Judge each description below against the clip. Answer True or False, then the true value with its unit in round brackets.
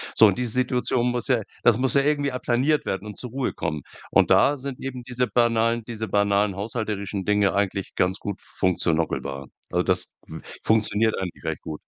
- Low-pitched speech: True (110 Hz)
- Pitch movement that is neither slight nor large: True (3.9 semitones)